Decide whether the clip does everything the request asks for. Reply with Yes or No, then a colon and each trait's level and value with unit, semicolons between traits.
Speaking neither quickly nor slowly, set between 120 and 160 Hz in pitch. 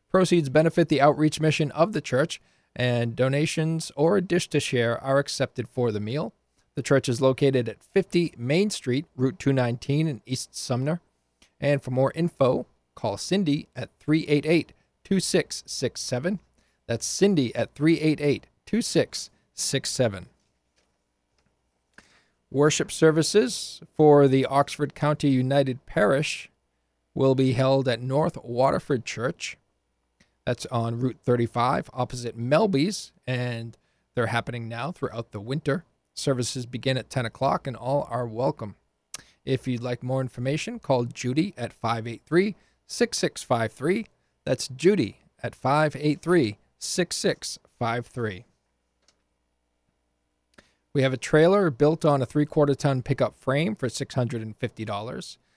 No: slow, 120 wpm; low, 135 Hz